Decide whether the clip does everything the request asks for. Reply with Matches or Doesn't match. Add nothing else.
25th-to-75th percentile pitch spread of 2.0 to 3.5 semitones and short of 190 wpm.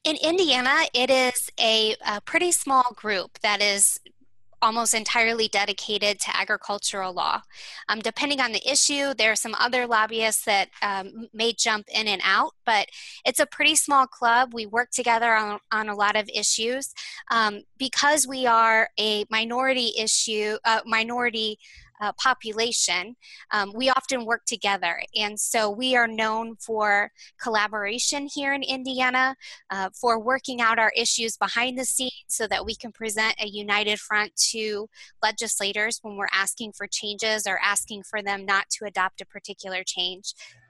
Matches